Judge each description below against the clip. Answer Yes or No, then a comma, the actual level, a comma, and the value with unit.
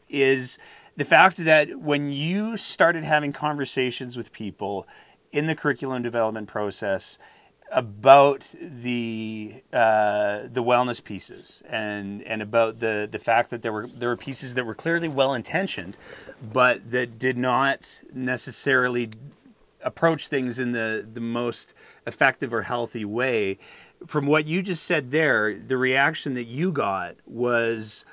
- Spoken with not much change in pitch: No, average, 4.2 semitones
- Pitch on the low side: Yes, low, 125 Hz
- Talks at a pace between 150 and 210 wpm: No, average, 140 wpm